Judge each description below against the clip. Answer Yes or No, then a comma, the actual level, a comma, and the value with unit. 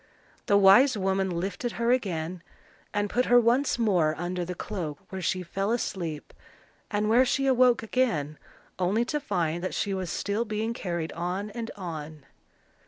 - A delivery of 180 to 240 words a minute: No, average, 165 wpm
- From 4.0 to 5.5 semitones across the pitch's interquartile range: Yes, average, 4.9 semitones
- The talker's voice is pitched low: No, high, 195 Hz